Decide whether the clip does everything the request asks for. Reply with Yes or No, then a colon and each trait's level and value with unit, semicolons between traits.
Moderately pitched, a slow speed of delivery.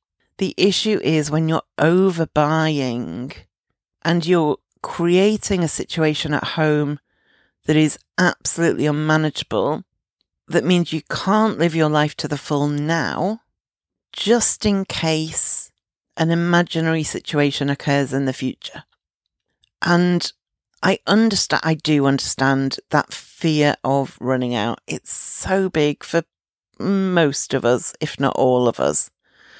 Yes: medium, 155 Hz; slow, 125 wpm